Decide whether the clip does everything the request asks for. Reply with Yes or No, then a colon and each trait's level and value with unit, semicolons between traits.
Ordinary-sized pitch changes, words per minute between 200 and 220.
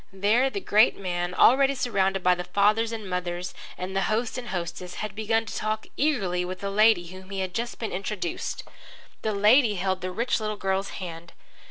Yes: average, 3.4 semitones; fast, 205 wpm